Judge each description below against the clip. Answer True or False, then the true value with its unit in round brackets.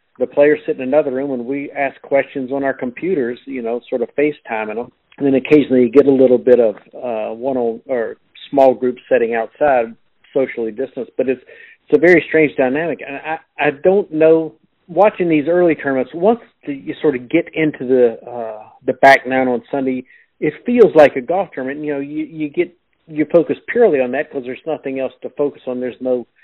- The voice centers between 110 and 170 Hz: True (140 Hz)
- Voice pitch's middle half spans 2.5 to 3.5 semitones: True (3.2 semitones)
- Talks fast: True (215 wpm)